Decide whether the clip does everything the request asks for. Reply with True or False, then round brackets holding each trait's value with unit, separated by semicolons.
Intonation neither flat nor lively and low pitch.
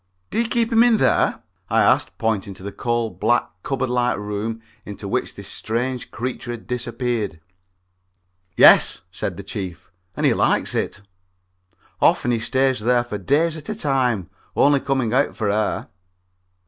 True (4.1 semitones; 120 Hz)